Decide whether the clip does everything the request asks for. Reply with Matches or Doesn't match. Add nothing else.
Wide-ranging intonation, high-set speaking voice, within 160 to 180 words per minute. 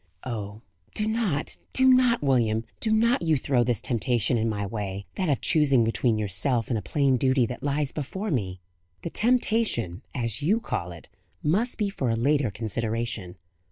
Doesn't match